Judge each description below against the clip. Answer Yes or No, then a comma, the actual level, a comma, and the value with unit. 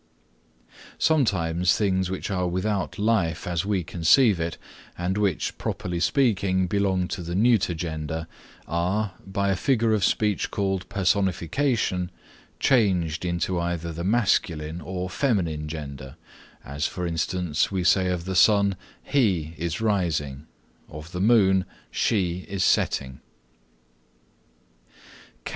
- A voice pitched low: Yes, very low, 90 Hz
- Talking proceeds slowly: Yes, slow, 120 wpm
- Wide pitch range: No, average, 3.1 semitones